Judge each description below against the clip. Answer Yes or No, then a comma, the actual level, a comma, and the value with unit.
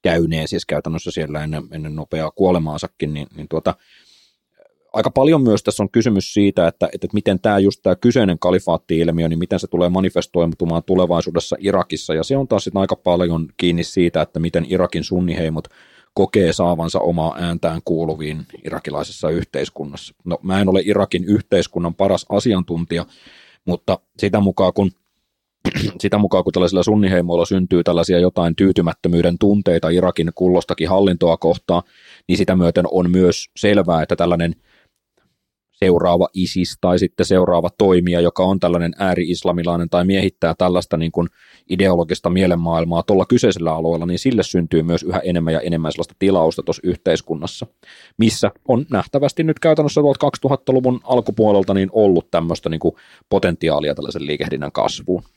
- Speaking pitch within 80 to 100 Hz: Yes, very low, 90 Hz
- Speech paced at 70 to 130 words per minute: No, average, 145 wpm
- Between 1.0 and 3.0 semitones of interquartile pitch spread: Yes, narrow, 2.5 semitones